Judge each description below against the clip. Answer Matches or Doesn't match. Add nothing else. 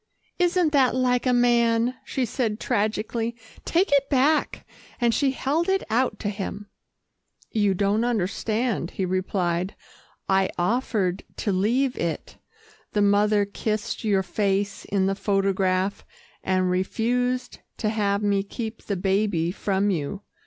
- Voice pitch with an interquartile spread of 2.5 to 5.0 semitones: Matches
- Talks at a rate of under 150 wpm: Matches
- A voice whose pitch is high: Matches